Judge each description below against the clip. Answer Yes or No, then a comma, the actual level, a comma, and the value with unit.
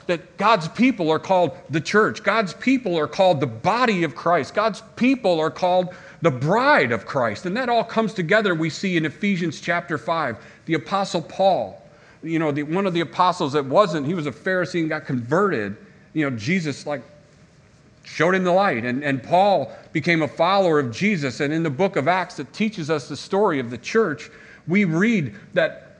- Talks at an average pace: Yes, average, 195 wpm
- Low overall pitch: No, medium, 170 Hz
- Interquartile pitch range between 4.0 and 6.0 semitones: Yes, average, 4.4 semitones